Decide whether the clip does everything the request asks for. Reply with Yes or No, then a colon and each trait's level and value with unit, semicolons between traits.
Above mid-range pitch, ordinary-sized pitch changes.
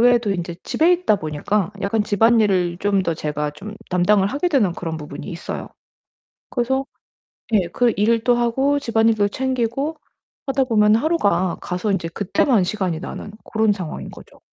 Yes: high, 210 Hz; average, 4.9 semitones